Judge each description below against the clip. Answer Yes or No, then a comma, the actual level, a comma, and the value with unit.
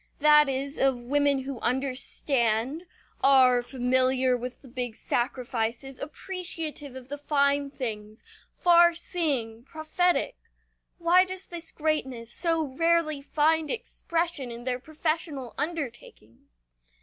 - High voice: Yes, very high, 275 Hz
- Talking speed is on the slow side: Yes, slow, 115 wpm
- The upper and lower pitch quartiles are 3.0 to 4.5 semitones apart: Yes, average, 4.2 semitones